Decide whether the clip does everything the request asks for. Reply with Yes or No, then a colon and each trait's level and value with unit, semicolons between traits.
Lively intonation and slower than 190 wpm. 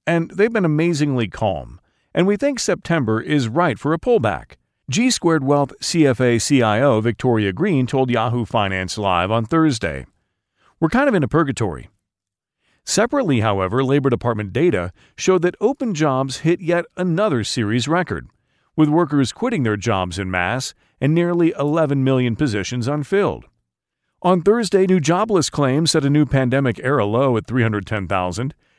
Yes: wide, 7.1 semitones; average, 150 wpm